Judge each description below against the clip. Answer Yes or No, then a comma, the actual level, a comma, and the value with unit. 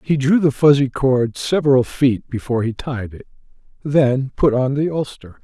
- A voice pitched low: Yes, low, 130 Hz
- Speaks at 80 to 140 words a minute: No, average, 175 wpm